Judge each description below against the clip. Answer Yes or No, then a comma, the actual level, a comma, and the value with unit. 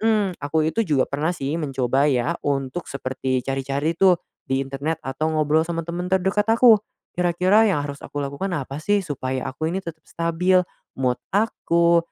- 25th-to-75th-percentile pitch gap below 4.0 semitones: No, average, 4.7 semitones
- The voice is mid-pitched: Yes, medium, 160 Hz